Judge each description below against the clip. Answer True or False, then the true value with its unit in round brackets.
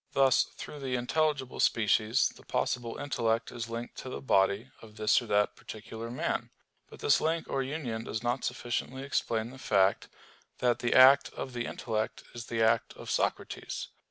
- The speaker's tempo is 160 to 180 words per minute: True (175 wpm)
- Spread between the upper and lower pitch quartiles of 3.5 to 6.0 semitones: False (2.8 semitones)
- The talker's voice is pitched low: True (120 Hz)